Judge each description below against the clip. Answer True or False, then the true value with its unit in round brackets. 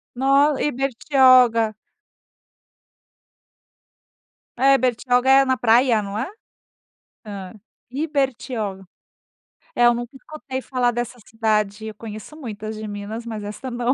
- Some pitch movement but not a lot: True (3.4 semitones)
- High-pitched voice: True (240 Hz)